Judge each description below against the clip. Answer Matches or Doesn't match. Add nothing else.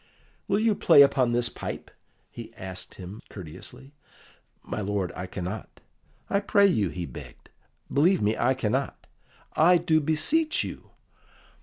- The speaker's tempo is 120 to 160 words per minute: Matches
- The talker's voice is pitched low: Matches